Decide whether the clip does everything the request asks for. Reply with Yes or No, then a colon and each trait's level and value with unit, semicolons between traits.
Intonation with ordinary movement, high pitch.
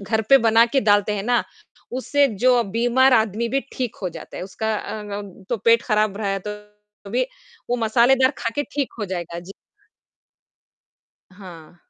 Yes: average, 3.3 semitones; high, 220 Hz